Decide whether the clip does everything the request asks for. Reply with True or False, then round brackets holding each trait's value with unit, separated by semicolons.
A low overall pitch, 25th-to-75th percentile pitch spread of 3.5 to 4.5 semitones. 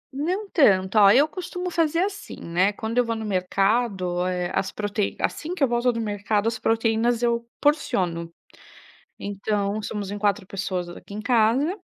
False (215 Hz; 4.0 semitones)